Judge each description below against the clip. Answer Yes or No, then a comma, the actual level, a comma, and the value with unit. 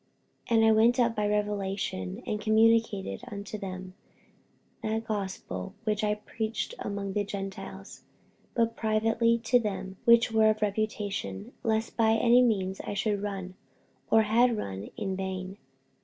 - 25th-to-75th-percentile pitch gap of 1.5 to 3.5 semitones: Yes, narrow, 2.5 semitones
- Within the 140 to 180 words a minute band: Yes, average, 145 wpm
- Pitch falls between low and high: No, high, 210 Hz